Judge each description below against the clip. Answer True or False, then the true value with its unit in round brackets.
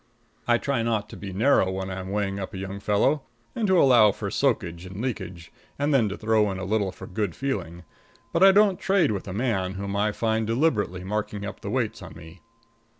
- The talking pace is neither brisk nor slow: False (215 wpm)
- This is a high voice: False (105 Hz)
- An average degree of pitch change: True (4.3 semitones)